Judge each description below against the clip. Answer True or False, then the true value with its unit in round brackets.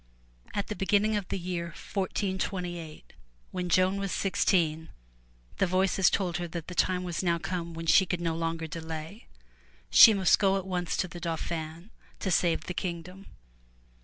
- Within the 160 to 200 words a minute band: True (165 wpm)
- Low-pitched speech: False (180 Hz)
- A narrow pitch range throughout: True (2.3 semitones)